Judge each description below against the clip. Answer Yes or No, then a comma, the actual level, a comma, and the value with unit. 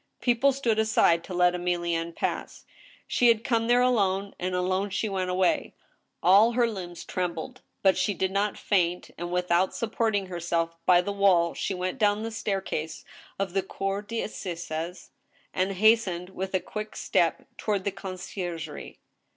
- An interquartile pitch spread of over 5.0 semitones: No, average, 3.2 semitones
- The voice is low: No, high, 190 Hz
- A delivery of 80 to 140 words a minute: No, average, 160 wpm